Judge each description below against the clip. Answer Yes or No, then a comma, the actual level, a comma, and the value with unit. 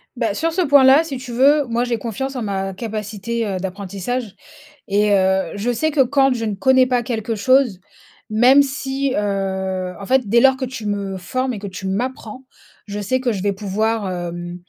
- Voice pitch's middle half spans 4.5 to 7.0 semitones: Yes, average, 4.8 semitones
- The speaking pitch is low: No, high, 225 Hz